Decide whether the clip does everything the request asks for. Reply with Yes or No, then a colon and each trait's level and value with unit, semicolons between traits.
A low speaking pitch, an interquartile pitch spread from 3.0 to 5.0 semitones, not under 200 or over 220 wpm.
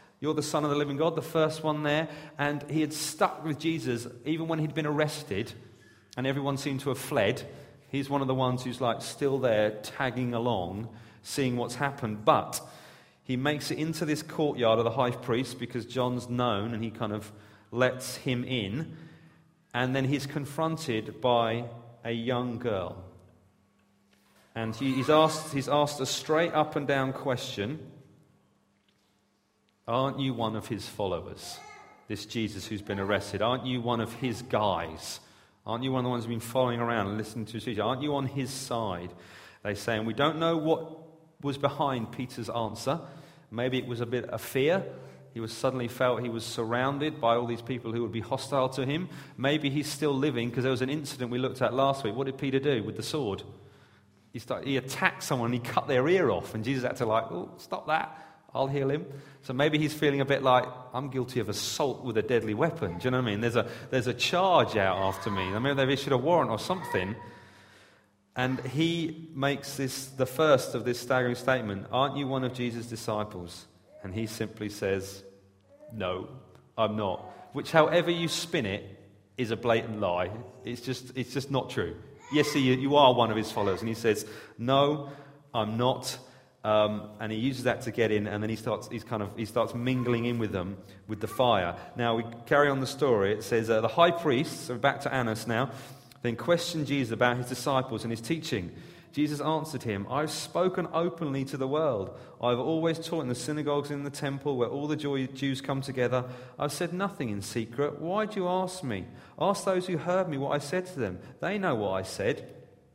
Yes: low, 130 Hz; average, 4.2 semitones; fast, 205 wpm